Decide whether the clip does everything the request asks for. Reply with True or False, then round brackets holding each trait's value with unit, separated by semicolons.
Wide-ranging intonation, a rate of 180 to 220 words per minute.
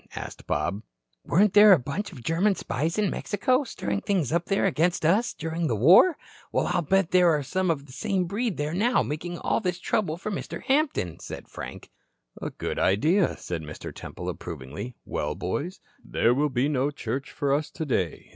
True (6.6 semitones; 190 wpm)